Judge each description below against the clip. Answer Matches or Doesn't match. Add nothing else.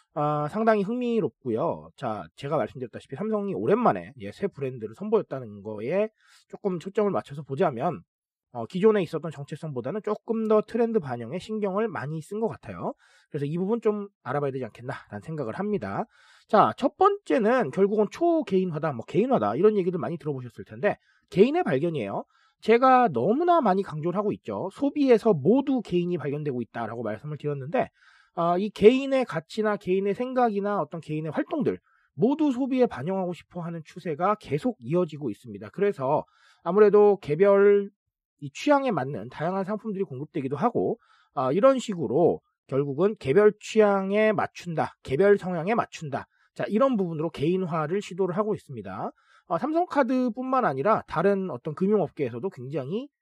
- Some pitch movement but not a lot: Doesn't match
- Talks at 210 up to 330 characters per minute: Doesn't match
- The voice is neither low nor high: Doesn't match